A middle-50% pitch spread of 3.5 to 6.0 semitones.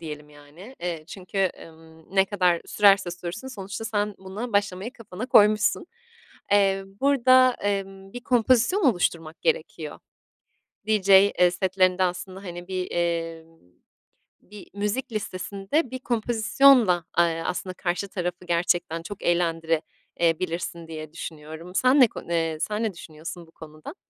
Yes: average, 3.8 semitones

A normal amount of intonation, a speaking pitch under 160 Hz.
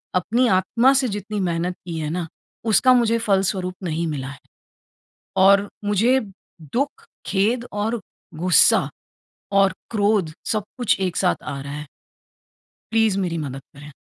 No: average, 4.8 semitones; high, 195 Hz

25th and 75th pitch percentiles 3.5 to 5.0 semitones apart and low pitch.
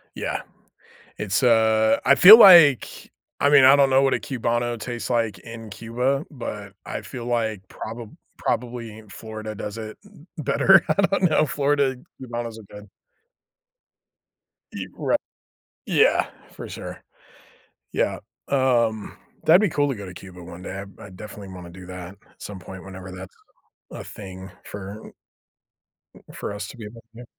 Yes: average, 4.5 semitones; low, 115 Hz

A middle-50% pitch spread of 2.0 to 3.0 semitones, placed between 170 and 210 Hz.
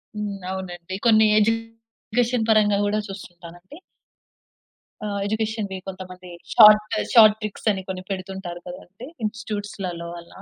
Yes: average, 2.7 semitones; high, 205 Hz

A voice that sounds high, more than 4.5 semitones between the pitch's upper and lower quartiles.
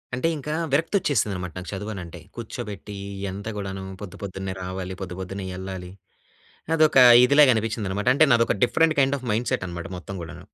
No: low, 100 Hz; average, 5.0 semitones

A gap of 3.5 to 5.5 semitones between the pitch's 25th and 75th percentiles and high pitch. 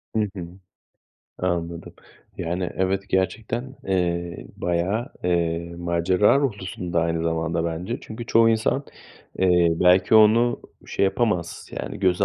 No: average, 3.8 semitones; very low, 90 Hz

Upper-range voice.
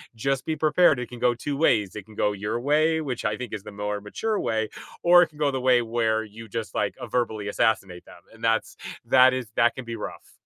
No: low, 120 Hz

